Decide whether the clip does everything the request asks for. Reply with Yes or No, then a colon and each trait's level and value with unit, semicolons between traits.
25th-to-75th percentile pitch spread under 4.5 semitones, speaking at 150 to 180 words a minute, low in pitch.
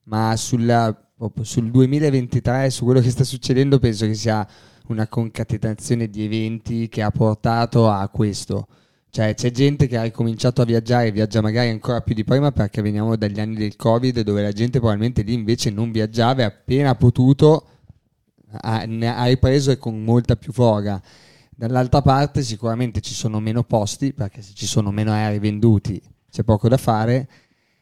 Yes: narrow, 2.5 semitones; fast, 170 wpm; low, 115 Hz